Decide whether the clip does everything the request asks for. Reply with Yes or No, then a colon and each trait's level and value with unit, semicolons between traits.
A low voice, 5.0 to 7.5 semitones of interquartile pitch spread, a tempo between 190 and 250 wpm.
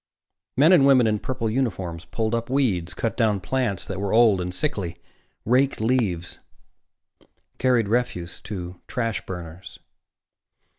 No: low, 110 Hz; wide, 5.5 semitones; slow, 135 wpm